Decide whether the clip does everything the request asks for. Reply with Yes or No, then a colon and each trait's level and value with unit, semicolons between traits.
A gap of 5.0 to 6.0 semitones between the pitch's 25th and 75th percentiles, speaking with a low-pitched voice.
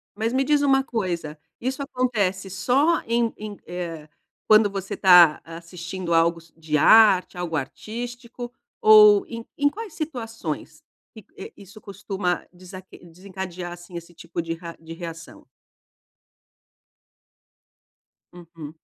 No: wide, 5.6 semitones; high, 190 Hz